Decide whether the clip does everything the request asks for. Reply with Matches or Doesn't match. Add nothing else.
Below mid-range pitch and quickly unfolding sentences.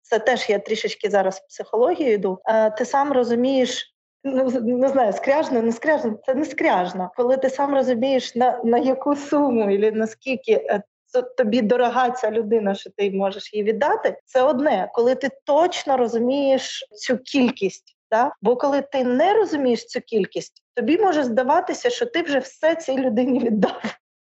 Doesn't match